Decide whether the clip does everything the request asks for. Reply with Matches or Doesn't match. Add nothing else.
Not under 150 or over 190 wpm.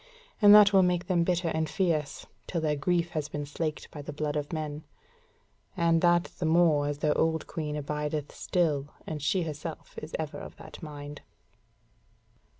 Matches